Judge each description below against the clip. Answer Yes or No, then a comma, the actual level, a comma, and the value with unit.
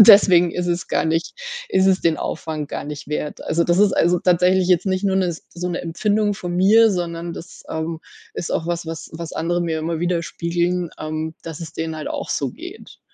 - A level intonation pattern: Yes, narrow, 1.9 semitones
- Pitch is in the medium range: Yes, medium, 170 Hz